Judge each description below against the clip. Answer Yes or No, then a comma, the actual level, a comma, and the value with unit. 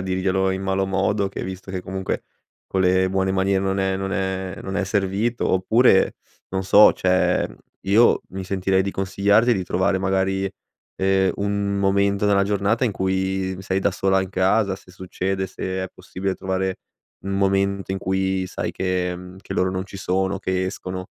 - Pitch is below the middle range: Yes, very low, 95 Hz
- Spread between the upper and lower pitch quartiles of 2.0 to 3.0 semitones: No, narrow, 0.7 semitones